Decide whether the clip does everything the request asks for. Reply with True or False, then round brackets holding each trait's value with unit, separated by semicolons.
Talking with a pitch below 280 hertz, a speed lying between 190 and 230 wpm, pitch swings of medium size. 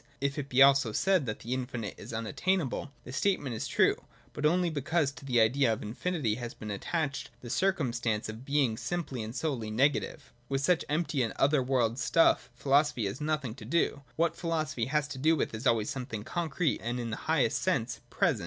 True (135 Hz; 200 wpm; 4.7 semitones)